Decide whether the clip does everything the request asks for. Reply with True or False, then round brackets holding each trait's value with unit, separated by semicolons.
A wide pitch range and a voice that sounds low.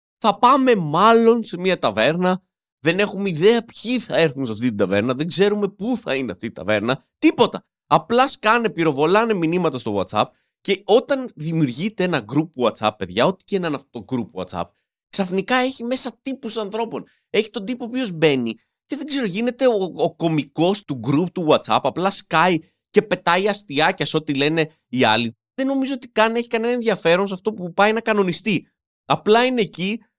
False (6.7 semitones; 190 Hz)